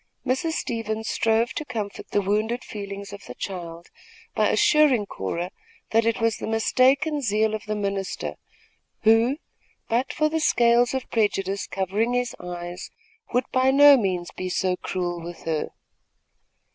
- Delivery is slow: No, average, 150 wpm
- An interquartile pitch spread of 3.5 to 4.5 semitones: Yes, average, 4.2 semitones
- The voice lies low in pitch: No, high, 220 Hz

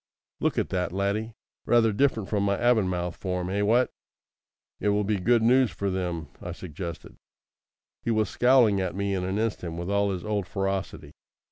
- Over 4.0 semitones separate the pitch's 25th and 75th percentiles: No, average, 3.1 semitones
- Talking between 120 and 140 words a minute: No, average, 175 wpm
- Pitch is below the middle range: Yes, low, 100 Hz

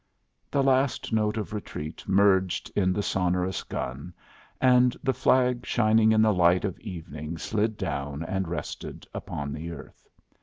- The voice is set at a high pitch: No, very low, 95 Hz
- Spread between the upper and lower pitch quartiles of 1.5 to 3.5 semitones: No, average, 4.6 semitones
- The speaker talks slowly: No, average, 150 wpm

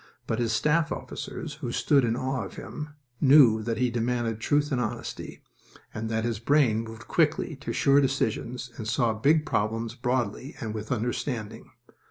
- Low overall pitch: Yes, low, 120 Hz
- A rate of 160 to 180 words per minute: Yes, average, 170 wpm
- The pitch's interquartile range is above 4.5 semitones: No, average, 3.9 semitones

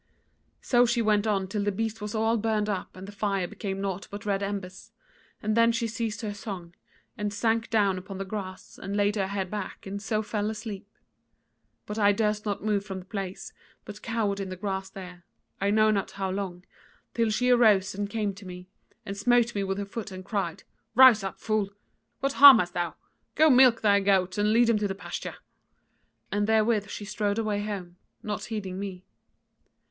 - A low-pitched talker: No, high, 205 Hz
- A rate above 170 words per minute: Yes, average, 200 wpm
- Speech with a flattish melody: Yes, narrow, 2.1 semitones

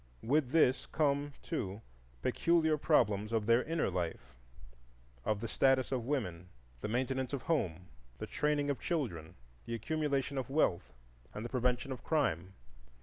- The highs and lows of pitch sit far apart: Yes, wide, 7.4 semitones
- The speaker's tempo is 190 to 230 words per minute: No, average, 145 wpm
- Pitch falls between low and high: No, low, 125 Hz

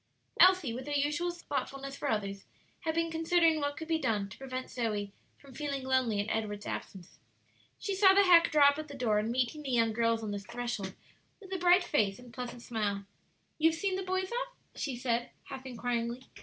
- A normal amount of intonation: No, wide, 6.0 semitones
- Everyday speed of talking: No, fast, 210 wpm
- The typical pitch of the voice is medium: No, very high, 260 Hz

